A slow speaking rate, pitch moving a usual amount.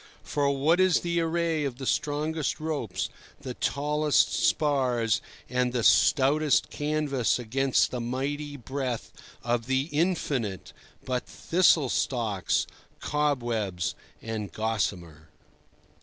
Yes: slow, 110 wpm; average, 4.2 semitones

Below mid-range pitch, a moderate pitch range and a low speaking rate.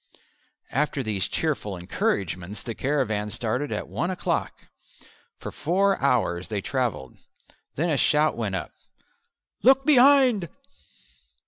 No: low, 130 Hz; wide, 8.8 semitones; slow, 115 wpm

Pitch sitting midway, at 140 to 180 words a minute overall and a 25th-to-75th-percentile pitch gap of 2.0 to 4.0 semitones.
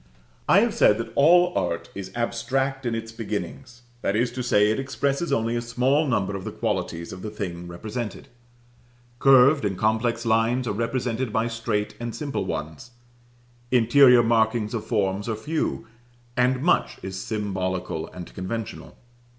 No: low, 115 Hz; average, 160 wpm; average, 3.5 semitones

